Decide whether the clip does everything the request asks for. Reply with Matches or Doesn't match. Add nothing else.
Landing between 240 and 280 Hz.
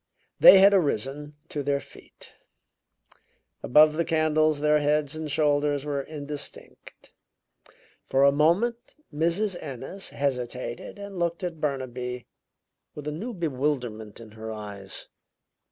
Doesn't match